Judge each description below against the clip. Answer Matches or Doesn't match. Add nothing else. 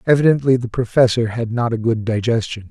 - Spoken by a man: Matches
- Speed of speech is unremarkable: Matches